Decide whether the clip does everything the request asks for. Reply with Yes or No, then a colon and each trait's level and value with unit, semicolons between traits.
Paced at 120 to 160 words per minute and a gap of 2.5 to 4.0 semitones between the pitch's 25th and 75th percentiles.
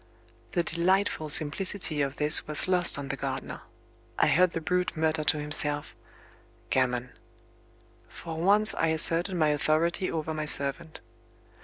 Yes: average, 140 wpm; average, 2.9 semitones